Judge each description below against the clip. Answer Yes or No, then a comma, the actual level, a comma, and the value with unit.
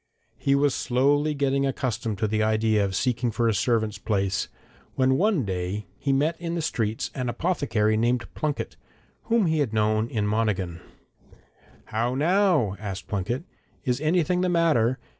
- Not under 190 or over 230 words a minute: No, average, 160 wpm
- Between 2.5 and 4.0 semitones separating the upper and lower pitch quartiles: No, average, 5.2 semitones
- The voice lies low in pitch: Yes, low, 120 Hz